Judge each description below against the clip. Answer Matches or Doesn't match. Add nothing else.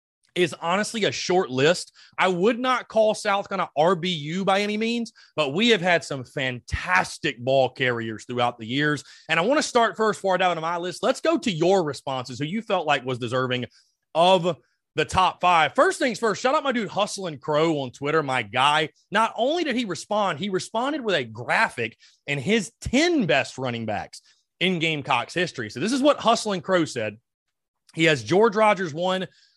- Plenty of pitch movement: Matches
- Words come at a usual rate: Matches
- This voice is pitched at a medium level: Matches